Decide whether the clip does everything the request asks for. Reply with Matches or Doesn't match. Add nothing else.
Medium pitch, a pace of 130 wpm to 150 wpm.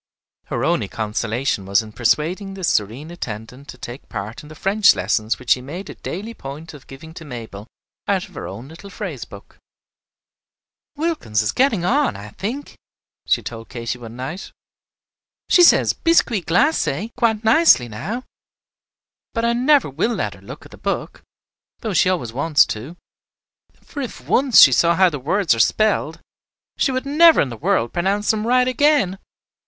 Doesn't match